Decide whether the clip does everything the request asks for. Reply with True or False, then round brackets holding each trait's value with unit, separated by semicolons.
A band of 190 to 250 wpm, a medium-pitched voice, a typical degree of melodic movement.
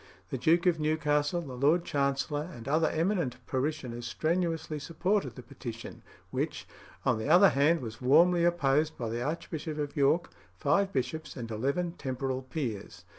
False (155 wpm; 150 Hz; 4.5 semitones)